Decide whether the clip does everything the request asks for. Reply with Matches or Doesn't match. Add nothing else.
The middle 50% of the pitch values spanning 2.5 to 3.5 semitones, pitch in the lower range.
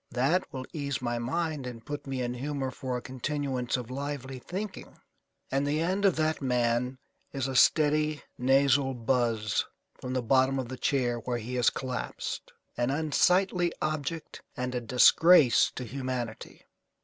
Matches